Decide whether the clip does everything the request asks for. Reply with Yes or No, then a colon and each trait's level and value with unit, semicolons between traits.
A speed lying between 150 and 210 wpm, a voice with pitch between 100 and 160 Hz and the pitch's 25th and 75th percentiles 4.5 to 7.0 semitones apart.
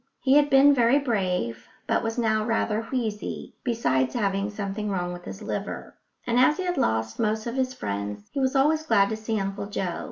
No: average, 200 wpm; high, 220 Hz; average, 4.8 semitones